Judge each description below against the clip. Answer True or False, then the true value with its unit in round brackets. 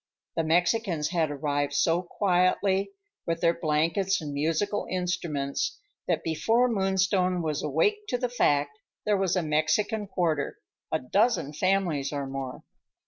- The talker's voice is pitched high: False (170 Hz)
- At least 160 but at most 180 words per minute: False (140 wpm)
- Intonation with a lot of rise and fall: False (4.4 semitones)